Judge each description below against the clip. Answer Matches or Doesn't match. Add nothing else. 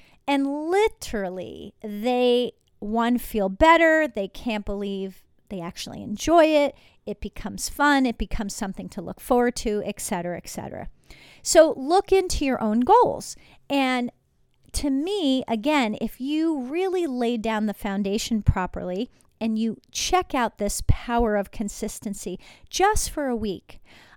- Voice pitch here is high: Matches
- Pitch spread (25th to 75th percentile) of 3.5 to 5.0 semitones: Doesn't match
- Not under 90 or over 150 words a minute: Matches